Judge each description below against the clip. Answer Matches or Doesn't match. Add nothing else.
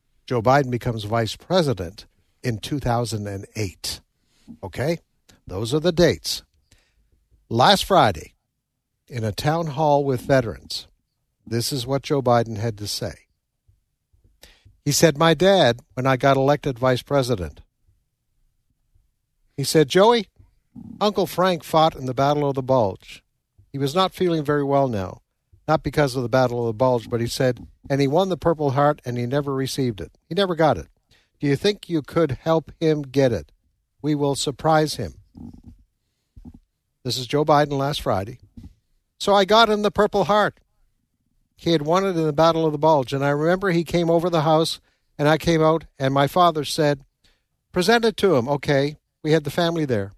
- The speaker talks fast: Doesn't match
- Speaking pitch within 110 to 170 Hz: Matches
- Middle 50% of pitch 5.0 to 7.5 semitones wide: Matches